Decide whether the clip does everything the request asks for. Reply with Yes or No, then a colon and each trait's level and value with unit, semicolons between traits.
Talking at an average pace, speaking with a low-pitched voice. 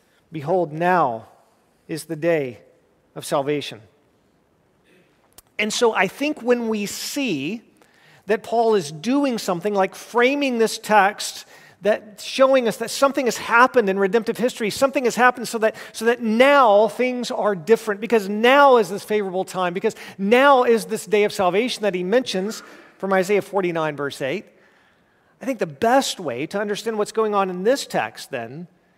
No: average, 165 wpm; high, 215 Hz